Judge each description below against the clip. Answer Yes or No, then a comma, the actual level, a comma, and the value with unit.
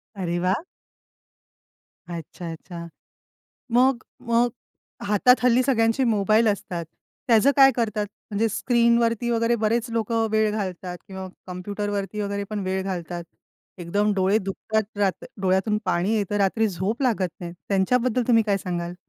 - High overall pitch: Yes, high, 205 Hz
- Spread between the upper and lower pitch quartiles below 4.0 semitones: Yes, average, 3.5 semitones